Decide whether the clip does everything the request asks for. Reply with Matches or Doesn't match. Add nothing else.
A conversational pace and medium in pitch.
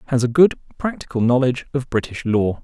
Doesn't match